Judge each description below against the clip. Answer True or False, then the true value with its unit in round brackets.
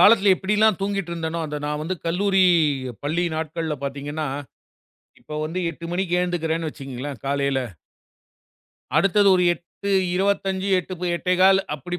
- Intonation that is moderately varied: True (3.9 semitones)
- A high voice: False (175 Hz)